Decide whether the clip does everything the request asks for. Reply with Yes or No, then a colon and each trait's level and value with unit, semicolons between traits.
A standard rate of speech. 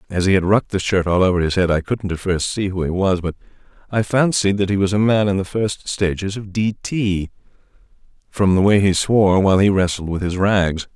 No: fast, 240 wpm